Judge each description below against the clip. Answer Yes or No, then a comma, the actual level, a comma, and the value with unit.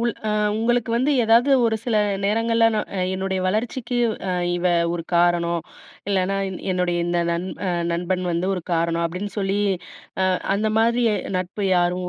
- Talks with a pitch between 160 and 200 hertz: Yes, high, 190 Hz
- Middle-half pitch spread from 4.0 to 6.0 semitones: Yes, average, 4.5 semitones